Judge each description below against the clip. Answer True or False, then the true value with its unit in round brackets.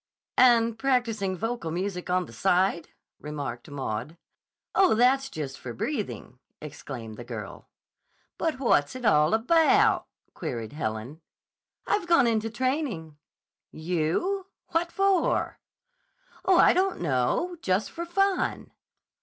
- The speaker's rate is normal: False (120 wpm)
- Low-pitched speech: False (205 Hz)